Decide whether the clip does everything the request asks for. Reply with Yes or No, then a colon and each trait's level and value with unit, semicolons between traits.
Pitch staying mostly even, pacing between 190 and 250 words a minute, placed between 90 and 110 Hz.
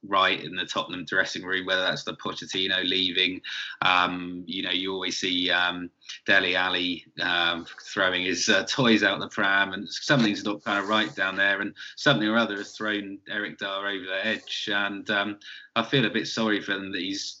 Yes: narrow, 2.1 semitones; average, 200 wpm; low, 100 Hz